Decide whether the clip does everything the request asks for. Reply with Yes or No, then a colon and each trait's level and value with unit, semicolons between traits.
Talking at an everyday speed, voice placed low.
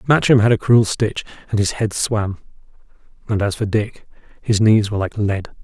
Yes: average, 190 wpm; low, 105 Hz